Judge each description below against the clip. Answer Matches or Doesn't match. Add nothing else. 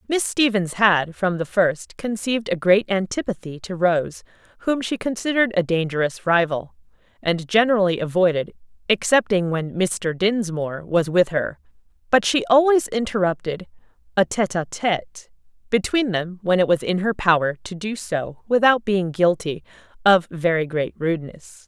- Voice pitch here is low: Doesn't match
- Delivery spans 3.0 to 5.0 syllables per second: Matches